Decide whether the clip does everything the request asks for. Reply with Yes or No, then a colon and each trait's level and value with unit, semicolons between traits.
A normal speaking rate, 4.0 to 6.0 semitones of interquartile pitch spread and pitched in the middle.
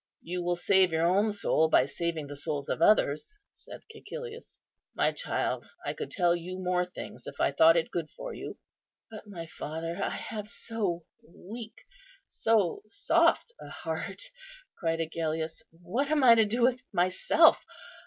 Yes: average, 165 wpm; average, 5.3 semitones; medium, 180 Hz